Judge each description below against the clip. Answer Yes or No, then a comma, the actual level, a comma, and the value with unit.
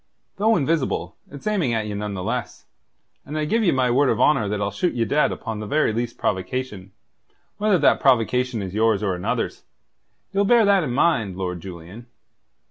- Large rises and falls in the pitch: Yes, wide, 6.9 semitones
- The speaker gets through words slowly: No, average, 195 wpm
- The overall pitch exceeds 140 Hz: No, low, 120 Hz